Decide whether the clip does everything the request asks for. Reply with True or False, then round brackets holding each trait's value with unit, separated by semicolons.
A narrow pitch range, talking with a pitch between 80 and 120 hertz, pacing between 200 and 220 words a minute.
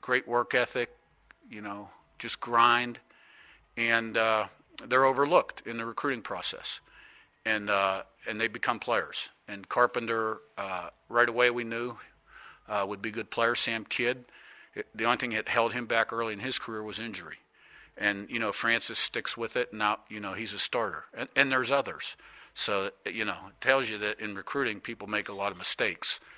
False (2.3 semitones; 115 Hz; 185 wpm)